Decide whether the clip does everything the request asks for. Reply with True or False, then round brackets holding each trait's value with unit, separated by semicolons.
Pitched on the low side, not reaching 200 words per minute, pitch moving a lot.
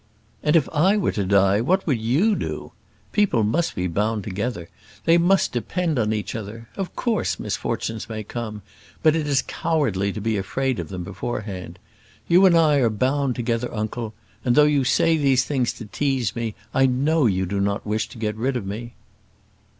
True (120 Hz; 190 wpm; 5.8 semitones)